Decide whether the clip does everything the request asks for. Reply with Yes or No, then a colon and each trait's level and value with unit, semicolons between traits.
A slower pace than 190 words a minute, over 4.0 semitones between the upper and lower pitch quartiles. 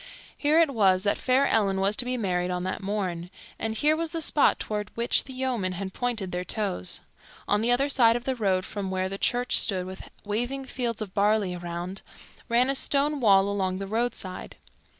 No: fast, 205 wpm; average, 4.7 semitones